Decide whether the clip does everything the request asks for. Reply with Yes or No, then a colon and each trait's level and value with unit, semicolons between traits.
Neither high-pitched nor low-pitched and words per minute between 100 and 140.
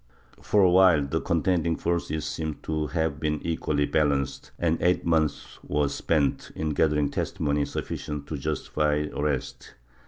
No: very low, 75 Hz; slow, 135 wpm